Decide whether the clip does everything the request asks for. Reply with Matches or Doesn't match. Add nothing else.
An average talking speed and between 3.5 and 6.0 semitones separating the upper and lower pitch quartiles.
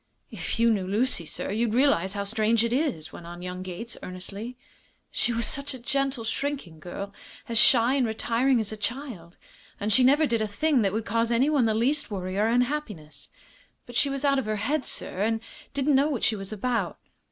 Doesn't match